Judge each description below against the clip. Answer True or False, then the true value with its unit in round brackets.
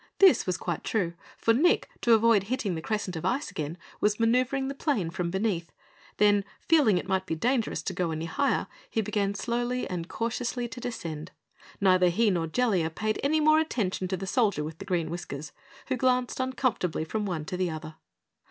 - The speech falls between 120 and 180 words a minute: False (190 wpm)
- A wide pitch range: True (5.9 semitones)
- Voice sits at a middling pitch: False (200 Hz)